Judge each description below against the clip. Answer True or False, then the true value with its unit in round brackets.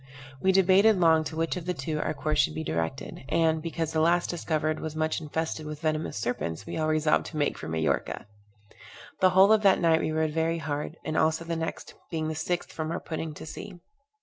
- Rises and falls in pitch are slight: True (1.6 semitones)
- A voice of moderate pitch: True (160 Hz)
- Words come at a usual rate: False (220 wpm)